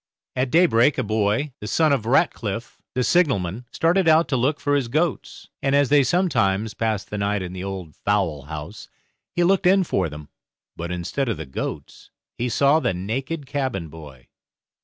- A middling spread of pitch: No, wide, 7.0 semitones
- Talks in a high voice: No, low, 115 Hz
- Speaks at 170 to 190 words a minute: Yes, average, 180 wpm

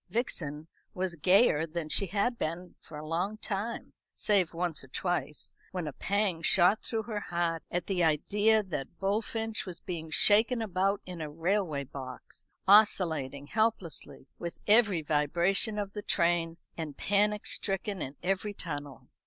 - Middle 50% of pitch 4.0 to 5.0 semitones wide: Yes, average, 4.3 semitones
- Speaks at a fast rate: No, average, 155 wpm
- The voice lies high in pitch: No, medium, 180 Hz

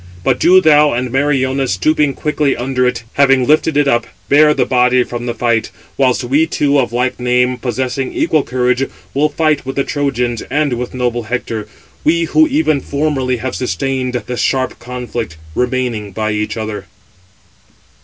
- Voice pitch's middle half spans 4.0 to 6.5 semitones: No, average, 2.8 semitones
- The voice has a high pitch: No, low, 130 Hz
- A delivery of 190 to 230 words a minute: No, average, 165 wpm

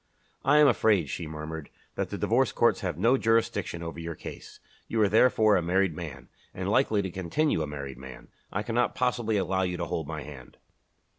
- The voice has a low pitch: Yes, very low, 90 Hz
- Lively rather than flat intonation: Yes, wide, 6.1 semitones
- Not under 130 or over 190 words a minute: No, average, 200 wpm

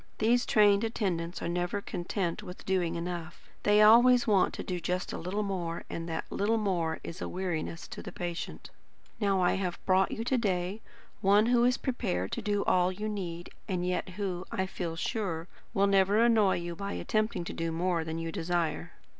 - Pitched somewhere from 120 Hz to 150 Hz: No, high, 190 Hz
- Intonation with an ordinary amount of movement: Yes, average, 3.3 semitones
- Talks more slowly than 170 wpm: No, average, 190 wpm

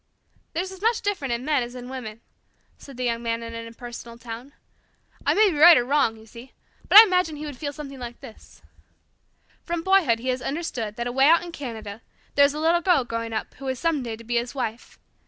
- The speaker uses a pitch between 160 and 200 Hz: No, very high, 255 Hz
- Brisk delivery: Yes, fast, 230 wpm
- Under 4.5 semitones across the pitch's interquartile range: No, average, 5.0 semitones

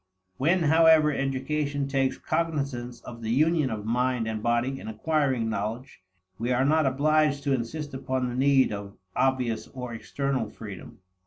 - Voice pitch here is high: No, low, 130 Hz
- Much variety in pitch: No, average, 3.6 semitones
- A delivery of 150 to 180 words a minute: Yes, average, 155 wpm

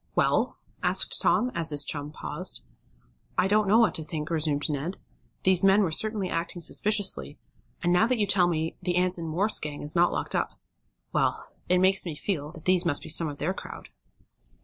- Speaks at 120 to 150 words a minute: No, average, 195 wpm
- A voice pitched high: No, medium, 175 Hz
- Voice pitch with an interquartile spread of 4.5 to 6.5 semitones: No, average, 3.7 semitones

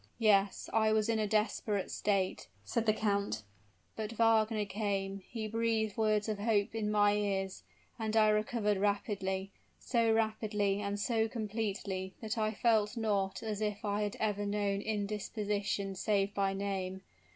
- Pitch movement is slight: Yes, narrow, 1.6 semitones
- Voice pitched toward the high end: Yes, high, 210 Hz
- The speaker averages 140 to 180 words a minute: Yes, average, 150 wpm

